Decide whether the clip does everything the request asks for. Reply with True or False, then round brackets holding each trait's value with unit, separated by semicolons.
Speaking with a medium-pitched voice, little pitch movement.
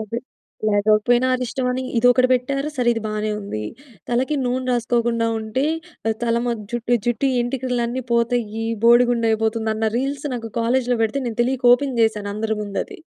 False (240 Hz; 2.1 semitones)